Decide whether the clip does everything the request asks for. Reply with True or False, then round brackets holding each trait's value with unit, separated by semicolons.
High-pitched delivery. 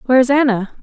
True (250 Hz)